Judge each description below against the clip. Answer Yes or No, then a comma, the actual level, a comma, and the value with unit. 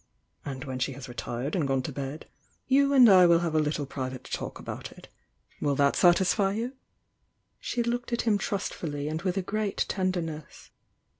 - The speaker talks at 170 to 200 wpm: Yes, average, 175 wpm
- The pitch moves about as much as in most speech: No, wide, 6.2 semitones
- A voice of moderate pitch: Yes, medium, 165 Hz